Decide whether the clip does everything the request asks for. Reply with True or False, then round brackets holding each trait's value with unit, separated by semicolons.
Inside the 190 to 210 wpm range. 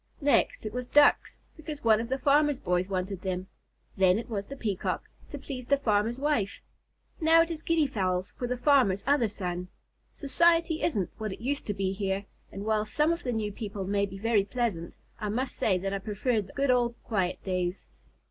True (205 wpm)